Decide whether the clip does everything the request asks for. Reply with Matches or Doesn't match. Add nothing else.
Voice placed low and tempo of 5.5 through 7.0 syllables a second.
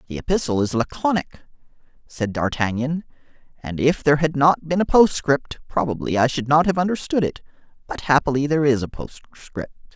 Doesn't match